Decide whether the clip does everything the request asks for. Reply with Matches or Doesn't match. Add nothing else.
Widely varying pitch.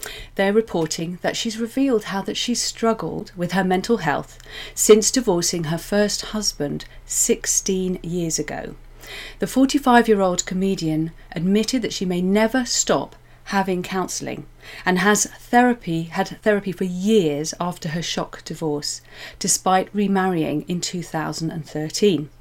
Doesn't match